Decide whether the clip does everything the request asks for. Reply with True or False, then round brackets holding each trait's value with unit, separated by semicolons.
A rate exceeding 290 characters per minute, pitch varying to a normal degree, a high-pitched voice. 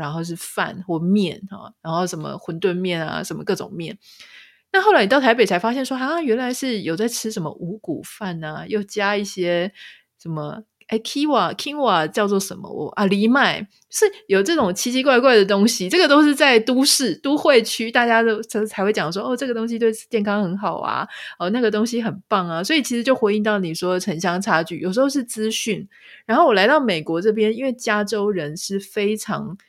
True (305 characters per minute; 4.9 semitones; 215 Hz)